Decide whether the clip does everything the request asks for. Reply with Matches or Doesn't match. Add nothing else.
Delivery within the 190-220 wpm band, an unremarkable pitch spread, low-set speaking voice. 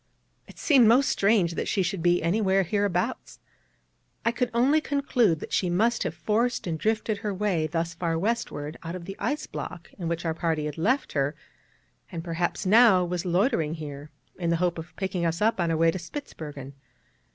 Doesn't match